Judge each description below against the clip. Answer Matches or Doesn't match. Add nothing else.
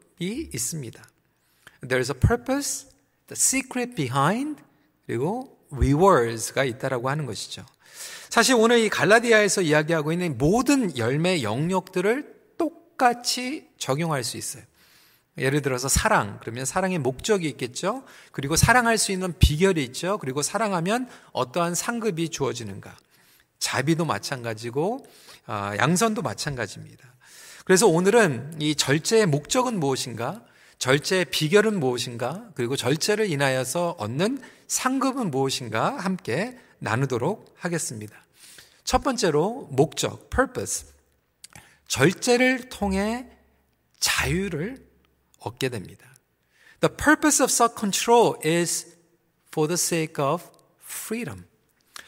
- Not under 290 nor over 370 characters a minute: Matches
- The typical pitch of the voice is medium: Matches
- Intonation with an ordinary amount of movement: Doesn't match